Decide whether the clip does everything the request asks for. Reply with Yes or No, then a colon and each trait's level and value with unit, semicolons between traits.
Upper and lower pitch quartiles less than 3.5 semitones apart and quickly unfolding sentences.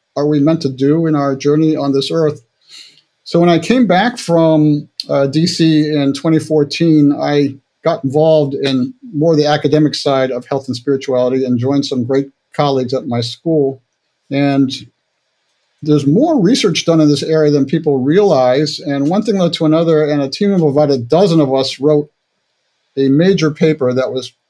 No: narrow, 2.6 semitones; average, 180 wpm